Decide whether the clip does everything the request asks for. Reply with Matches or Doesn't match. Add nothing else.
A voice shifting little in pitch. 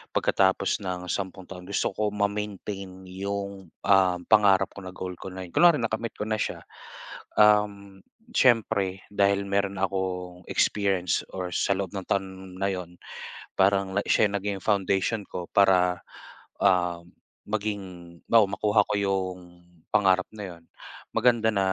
Matches